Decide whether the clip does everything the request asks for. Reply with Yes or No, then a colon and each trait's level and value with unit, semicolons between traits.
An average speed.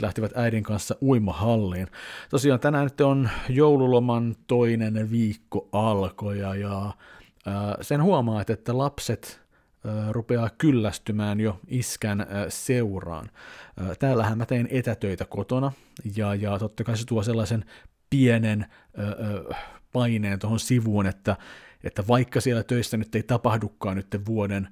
Yes: average, 110 wpm